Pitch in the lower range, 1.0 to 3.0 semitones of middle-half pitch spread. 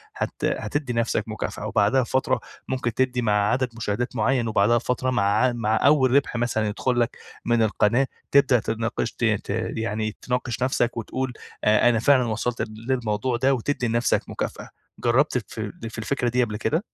Yes: low, 120 Hz; average, 2.7 semitones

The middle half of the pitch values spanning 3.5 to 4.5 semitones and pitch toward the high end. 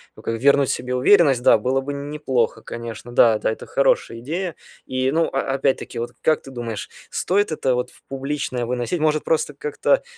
No: average, 3.9 semitones; low, 135 Hz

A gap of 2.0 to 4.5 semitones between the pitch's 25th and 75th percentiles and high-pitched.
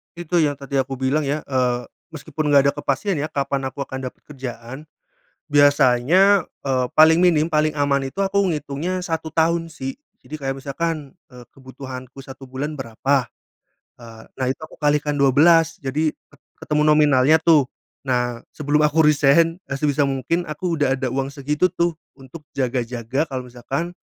No: average, 3.0 semitones; medium, 145 Hz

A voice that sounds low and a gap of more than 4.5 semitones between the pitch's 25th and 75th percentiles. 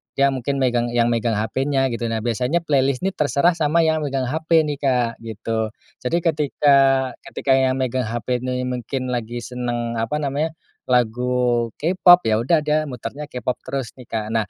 No: low, 130 Hz; average, 3.3 semitones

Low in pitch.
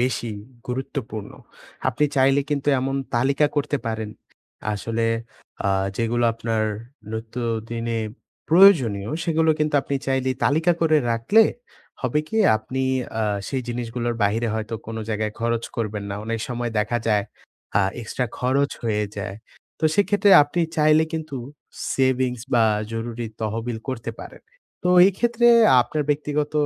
Yes: low, 120 Hz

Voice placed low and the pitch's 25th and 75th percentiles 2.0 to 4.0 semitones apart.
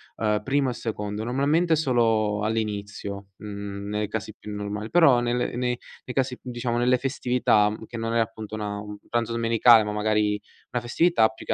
Yes: low, 115 Hz; average, 2.7 semitones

